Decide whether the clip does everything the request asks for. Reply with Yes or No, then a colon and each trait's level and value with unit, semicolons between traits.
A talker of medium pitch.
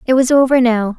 No: very high, 250 Hz